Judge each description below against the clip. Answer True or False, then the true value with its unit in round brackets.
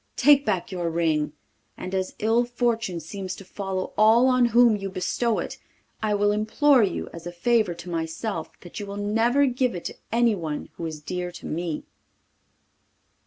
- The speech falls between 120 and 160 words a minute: False (175 wpm)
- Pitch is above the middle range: True (200 Hz)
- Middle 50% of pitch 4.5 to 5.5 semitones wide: True (5.1 semitones)